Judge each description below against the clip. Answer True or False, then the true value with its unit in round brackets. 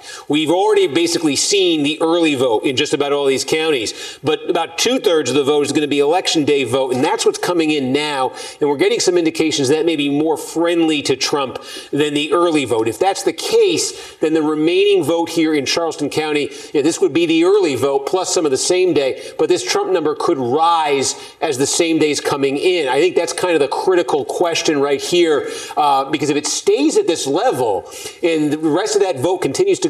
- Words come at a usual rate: False (225 wpm)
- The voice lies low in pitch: False (370 Hz)